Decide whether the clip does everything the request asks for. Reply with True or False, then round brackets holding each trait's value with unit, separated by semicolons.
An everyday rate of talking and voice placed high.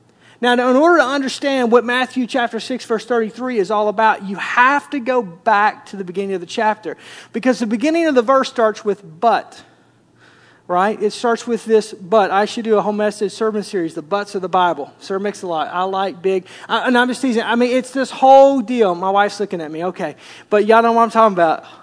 False (235 wpm; 220 Hz)